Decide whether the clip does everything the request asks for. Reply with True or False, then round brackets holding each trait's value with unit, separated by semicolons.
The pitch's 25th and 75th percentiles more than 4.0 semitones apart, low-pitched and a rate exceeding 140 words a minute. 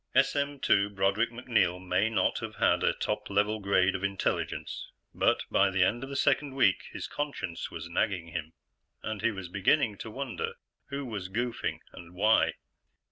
True (4.7 semitones; 105 Hz; 170 wpm)